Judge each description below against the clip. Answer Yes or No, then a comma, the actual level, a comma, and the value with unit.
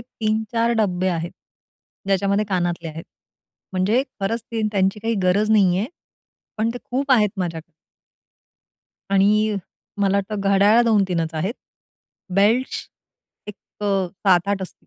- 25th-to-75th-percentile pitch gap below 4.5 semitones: Yes, average, 2.7 semitones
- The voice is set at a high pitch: Yes, high, 200 Hz